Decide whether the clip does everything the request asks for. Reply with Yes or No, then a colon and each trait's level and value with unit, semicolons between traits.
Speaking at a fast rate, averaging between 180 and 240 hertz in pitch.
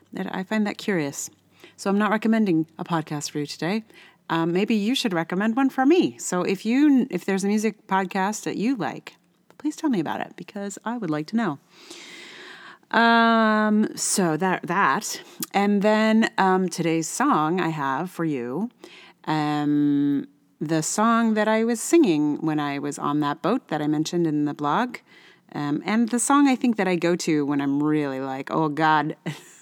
No: average, 185 wpm; high, 190 Hz